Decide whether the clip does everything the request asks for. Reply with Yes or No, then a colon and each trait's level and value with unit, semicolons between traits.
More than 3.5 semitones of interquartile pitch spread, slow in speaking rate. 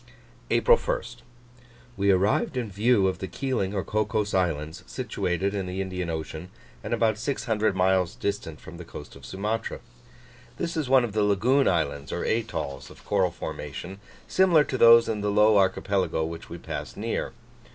No: average, 3.9 semitones; average, 170 wpm